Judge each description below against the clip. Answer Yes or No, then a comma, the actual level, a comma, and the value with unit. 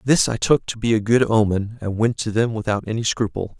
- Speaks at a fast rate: Yes, fast, 250 wpm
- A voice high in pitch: No, low, 110 Hz